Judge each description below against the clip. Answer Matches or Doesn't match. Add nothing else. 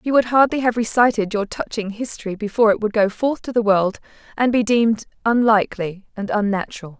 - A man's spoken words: Doesn't match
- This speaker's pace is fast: Doesn't match